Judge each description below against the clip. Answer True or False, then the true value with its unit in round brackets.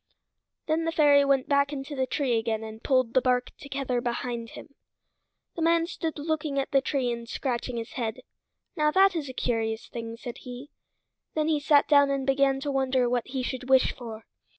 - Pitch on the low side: False (265 Hz)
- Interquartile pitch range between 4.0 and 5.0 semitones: False (3.1 semitones)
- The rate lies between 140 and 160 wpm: False (200 wpm)